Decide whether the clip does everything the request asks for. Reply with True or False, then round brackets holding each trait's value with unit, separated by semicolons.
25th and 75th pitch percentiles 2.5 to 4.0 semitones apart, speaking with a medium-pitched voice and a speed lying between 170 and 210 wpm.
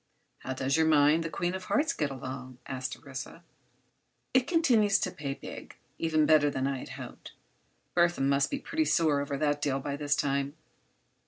True (3.5 semitones; 145 Hz; 175 wpm)